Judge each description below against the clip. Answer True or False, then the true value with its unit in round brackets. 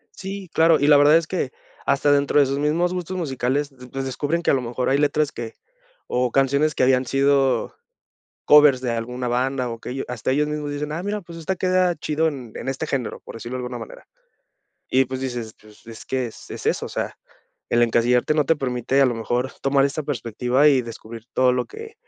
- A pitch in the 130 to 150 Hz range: True (135 Hz)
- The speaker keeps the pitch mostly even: False (3.3 semitones)